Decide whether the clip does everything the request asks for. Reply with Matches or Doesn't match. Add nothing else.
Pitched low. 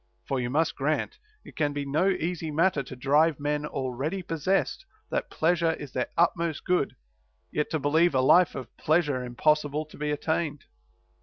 Doesn't match